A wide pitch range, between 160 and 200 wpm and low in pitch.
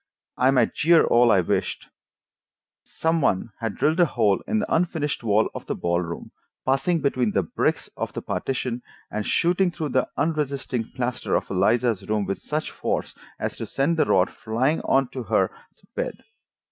Yes: wide, 5.9 semitones; average, 175 wpm; low, 130 Hz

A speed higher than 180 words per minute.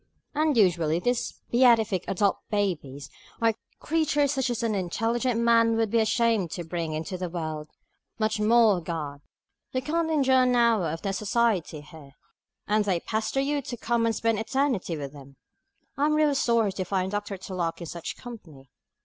No: average, 175 wpm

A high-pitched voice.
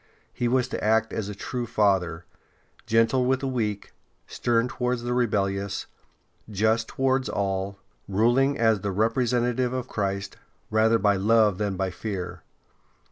No: low, 110 Hz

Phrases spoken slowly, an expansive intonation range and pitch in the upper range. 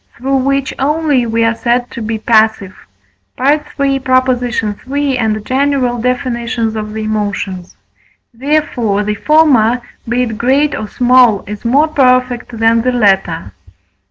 No: slow, 130 wpm; average, 3.2 semitones; high, 245 Hz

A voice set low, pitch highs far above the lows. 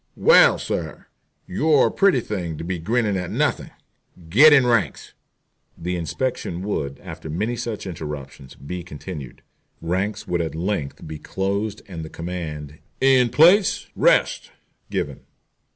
Yes: very low, 90 Hz; wide, 6.4 semitones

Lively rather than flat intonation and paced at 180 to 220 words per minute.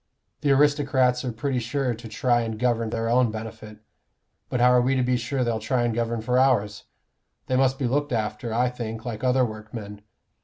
No: narrow, 2.4 semitones; fast, 205 wpm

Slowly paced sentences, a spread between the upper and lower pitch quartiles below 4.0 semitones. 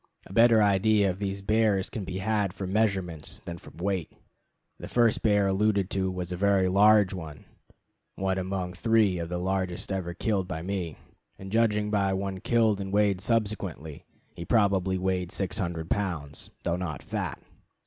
No: average, 170 wpm; narrow, 2.4 semitones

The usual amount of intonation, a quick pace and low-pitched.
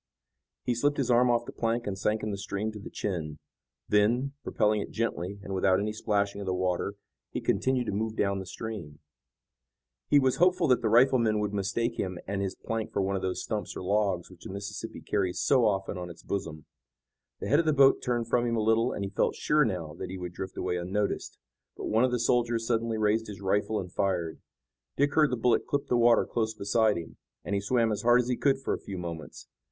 Yes: average, 3.5 semitones; fast, 230 wpm; low, 105 Hz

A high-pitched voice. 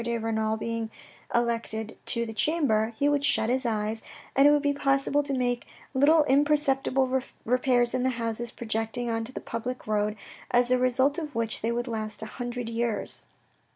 Yes: high, 240 Hz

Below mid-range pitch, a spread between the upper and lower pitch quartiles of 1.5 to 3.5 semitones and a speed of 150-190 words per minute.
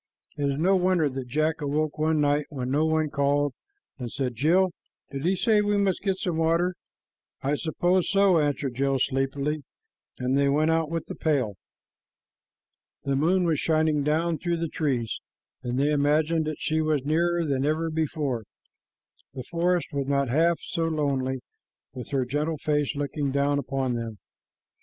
No: medium, 150 Hz; average, 3.0 semitones; average, 170 wpm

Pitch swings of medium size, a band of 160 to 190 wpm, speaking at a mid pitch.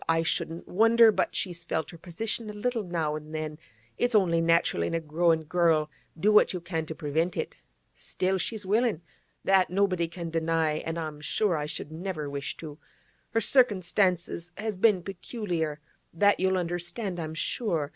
Yes: average, 3.7 semitones; average, 175 wpm; medium, 170 Hz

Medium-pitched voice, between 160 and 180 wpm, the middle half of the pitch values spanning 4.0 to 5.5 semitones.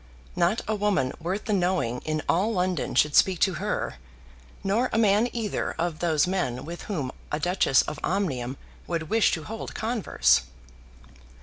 Yes: medium, 180 Hz; average, 165 wpm; average, 5.0 semitones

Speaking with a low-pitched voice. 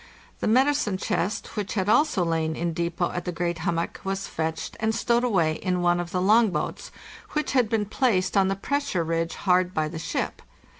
No: medium, 185 Hz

